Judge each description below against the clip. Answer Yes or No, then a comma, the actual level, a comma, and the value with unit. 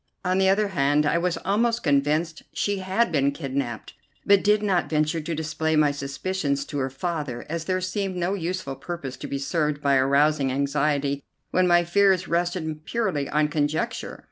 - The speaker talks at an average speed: Yes, average, 175 wpm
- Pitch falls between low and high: Yes, medium, 160 Hz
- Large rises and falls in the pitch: No, average, 4.6 semitones